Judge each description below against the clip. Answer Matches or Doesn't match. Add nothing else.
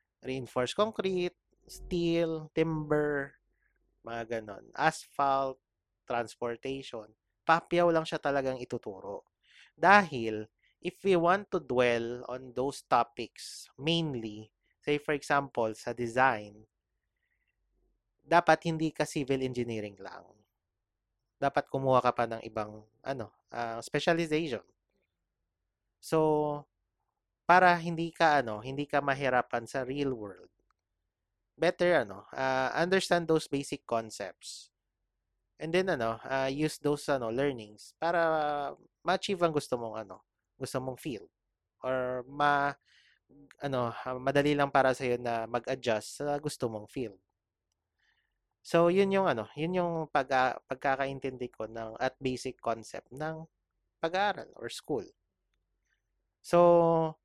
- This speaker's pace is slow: Matches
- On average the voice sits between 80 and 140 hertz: Matches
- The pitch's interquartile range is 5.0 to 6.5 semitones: Matches